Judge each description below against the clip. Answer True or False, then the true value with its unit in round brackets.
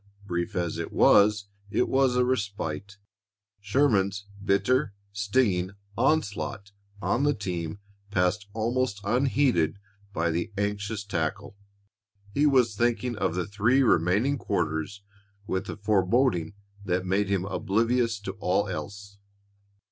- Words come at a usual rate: False (120 wpm)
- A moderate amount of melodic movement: True (4.0 semitones)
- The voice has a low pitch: True (100 Hz)